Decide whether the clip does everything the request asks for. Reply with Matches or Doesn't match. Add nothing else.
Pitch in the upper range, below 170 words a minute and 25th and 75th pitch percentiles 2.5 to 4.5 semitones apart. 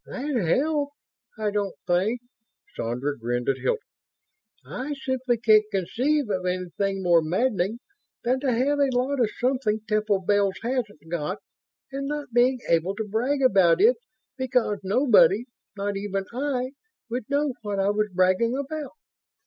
Doesn't match